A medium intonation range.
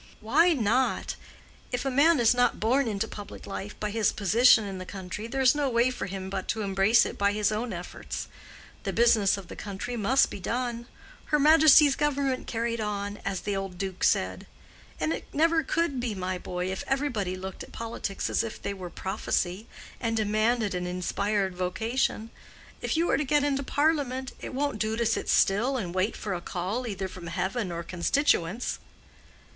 Yes: average, 4.9 semitones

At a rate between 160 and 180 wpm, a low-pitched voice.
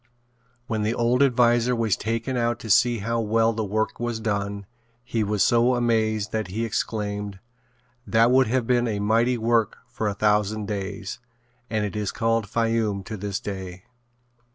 Yes: average, 170 wpm; low, 110 Hz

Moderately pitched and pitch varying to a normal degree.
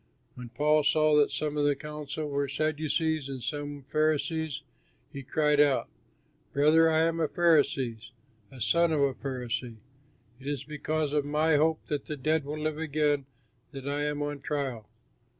No: medium, 150 Hz; narrow, 1.8 semitones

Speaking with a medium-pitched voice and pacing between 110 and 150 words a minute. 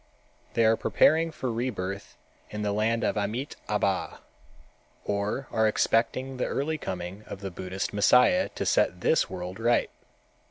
No: low, 110 Hz; average, 145 wpm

